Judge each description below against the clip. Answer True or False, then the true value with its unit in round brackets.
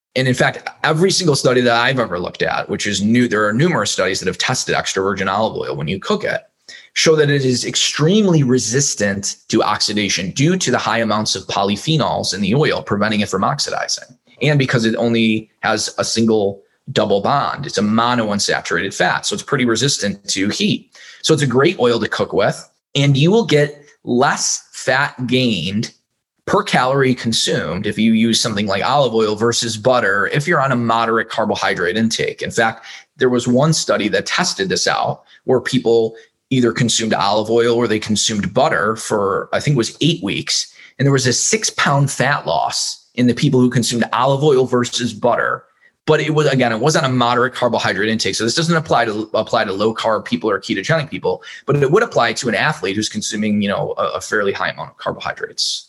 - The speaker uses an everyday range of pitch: True (4.0 semitones)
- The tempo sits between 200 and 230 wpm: True (205 wpm)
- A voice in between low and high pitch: False (120 Hz)